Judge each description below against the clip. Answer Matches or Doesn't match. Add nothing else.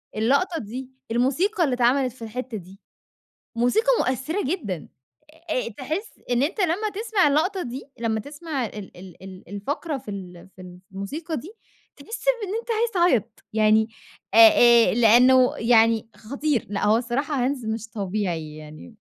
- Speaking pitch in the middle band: Doesn't match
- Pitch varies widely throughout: Matches